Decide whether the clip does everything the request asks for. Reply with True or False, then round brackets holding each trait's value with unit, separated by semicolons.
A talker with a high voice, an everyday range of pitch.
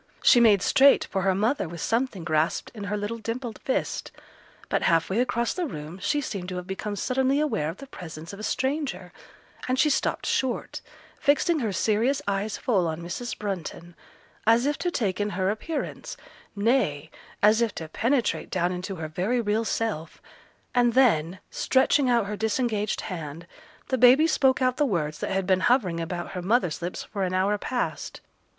False (210 Hz; 5.8 semitones)